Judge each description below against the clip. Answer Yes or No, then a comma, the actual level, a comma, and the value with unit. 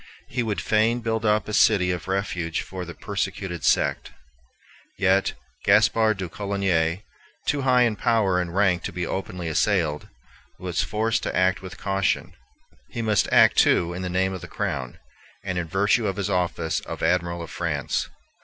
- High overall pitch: No, very low, 95 Hz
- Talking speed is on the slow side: No, average, 175 wpm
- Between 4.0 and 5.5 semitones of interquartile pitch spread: No, average, 3.2 semitones